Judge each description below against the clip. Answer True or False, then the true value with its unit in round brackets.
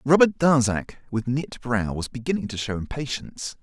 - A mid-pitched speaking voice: False (125 Hz)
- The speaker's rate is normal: True (165 wpm)